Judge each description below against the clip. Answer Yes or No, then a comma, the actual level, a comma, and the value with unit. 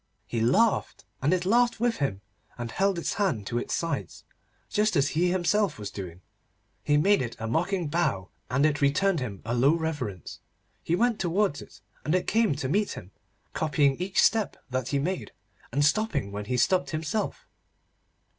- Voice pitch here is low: No, medium, 155 Hz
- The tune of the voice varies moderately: No, wide, 7.3 semitones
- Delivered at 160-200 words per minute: Yes, average, 180 wpm